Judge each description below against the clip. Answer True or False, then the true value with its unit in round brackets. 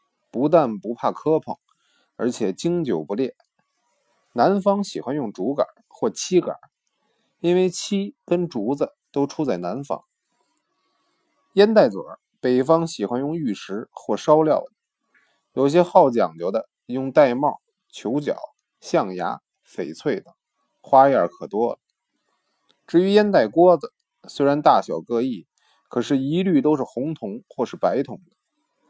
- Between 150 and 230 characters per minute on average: True (195 characters per minute)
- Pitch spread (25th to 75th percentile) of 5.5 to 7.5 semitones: True (6.0 semitones)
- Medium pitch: True (170 Hz)